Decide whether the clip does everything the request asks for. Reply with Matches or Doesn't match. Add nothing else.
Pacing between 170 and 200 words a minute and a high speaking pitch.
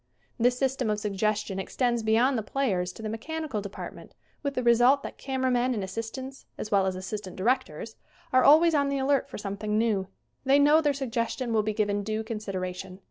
Matches